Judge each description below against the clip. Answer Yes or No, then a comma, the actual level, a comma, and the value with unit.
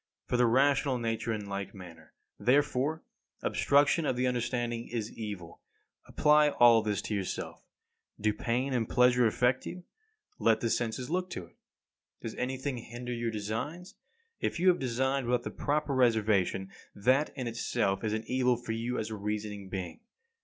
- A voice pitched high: No, low, 120 Hz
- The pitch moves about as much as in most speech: Yes, average, 3.3 semitones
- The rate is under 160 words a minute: No, average, 165 wpm